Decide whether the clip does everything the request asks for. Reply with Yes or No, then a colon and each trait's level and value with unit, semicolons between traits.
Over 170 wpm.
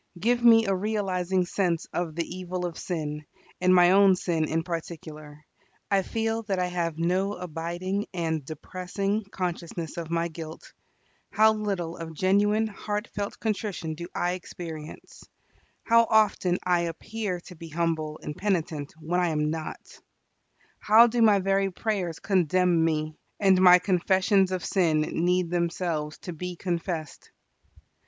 No: average, 145 wpm